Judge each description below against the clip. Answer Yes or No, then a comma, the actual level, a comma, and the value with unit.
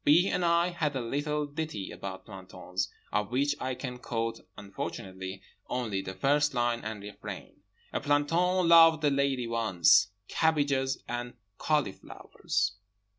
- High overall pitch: No, low, 130 Hz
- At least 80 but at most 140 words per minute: Yes, slow, 135 wpm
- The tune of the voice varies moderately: No, wide, 6.1 semitones